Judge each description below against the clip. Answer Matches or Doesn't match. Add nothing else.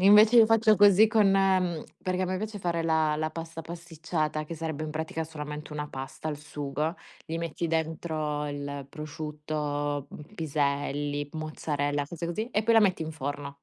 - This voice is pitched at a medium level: Matches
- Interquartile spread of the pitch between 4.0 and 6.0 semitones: Doesn't match